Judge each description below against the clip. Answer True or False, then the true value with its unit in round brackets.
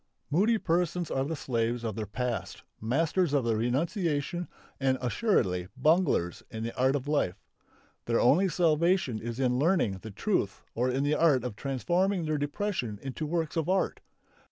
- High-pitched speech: False (140 Hz)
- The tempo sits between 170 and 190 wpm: False (160 wpm)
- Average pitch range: False (6.1 semitones)